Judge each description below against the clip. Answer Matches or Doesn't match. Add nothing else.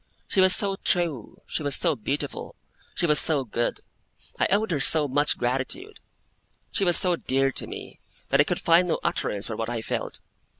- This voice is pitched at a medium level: Matches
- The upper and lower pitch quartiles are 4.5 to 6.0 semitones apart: Matches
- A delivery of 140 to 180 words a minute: Doesn't match